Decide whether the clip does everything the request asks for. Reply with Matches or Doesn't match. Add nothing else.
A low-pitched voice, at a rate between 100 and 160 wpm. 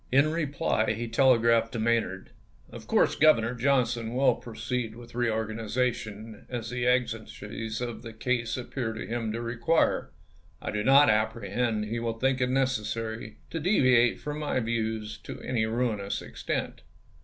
Matches